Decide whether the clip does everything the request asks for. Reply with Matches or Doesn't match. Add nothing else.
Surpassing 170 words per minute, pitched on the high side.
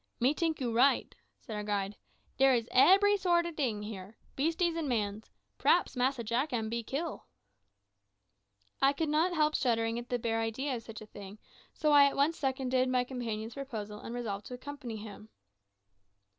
Matches